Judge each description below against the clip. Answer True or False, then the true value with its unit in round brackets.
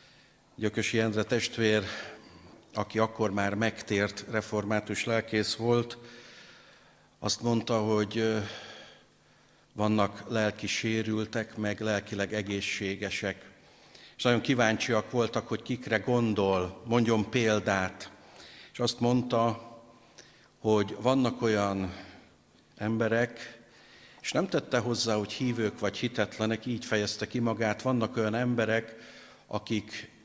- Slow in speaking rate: True (100 wpm)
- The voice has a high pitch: False (110 Hz)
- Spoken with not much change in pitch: True (1.7 semitones)